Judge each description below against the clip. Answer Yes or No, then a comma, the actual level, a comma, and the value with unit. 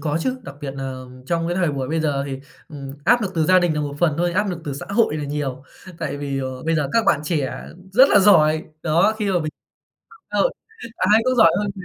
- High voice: No, medium, 160 Hz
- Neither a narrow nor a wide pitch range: Yes, average, 4.9 semitones